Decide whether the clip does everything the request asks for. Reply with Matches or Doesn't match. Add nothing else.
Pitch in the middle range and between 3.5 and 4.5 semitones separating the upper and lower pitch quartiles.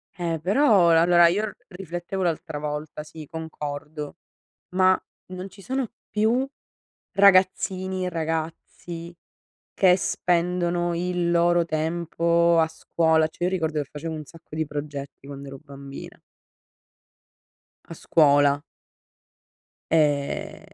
Doesn't match